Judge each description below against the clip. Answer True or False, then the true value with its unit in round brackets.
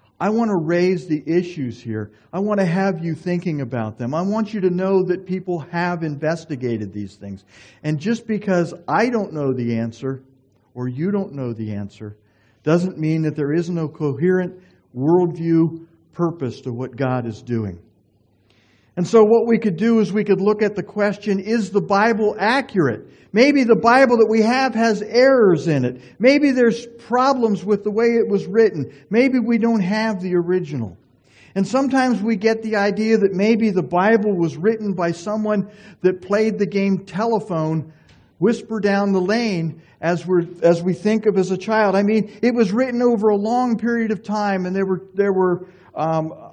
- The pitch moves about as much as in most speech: False (5.8 semitones)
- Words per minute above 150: True (185 wpm)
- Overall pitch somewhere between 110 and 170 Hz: False (185 Hz)